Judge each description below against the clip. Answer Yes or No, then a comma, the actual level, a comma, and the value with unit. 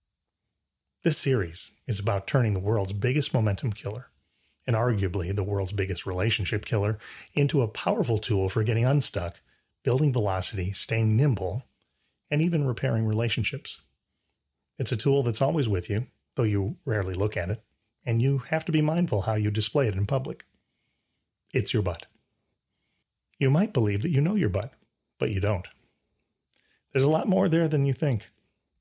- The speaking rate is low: No, average, 165 wpm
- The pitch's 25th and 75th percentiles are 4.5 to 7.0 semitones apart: Yes, wide, 5.5 semitones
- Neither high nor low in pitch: No, low, 110 Hz